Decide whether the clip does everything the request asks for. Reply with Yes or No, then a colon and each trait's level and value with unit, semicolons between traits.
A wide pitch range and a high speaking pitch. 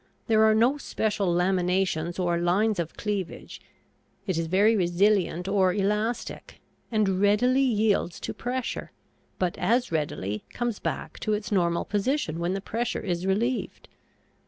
No: average, 3.7 semitones; high, 200 Hz